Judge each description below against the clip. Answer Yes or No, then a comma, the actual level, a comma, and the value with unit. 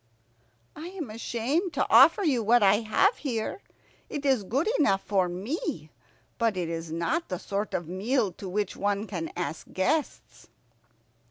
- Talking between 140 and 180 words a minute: Yes, average, 160 wpm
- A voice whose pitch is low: No, high, 215 Hz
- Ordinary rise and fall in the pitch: No, wide, 6.7 semitones